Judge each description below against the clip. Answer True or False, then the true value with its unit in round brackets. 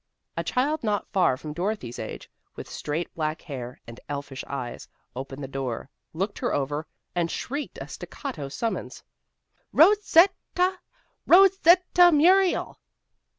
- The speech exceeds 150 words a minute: False (145 wpm)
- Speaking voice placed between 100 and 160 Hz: False (175 Hz)